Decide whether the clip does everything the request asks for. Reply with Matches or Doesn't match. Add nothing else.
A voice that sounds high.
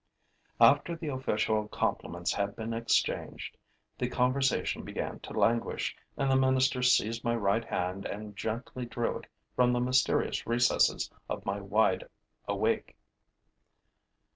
Doesn't match